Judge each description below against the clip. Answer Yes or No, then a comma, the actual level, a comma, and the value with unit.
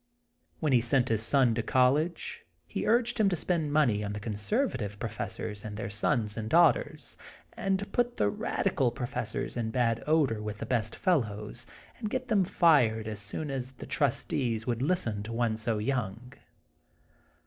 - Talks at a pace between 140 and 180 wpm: Yes, average, 175 wpm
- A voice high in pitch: No, low, 120 Hz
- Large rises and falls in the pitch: Yes, wide, 6.0 semitones